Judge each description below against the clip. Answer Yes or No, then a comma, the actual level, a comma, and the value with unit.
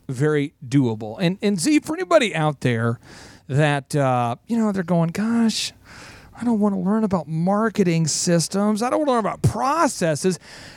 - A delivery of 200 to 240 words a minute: No, average, 175 wpm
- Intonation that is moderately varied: No, wide, 6.5 semitones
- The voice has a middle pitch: Yes, medium, 175 Hz